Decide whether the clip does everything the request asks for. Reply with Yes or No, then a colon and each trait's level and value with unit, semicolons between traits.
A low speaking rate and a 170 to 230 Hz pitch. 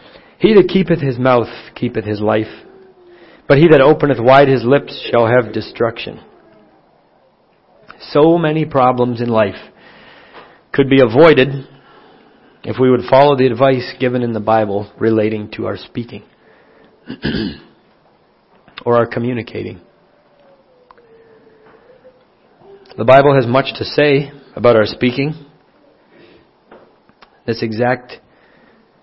No: slow, 110 wpm; low, 130 Hz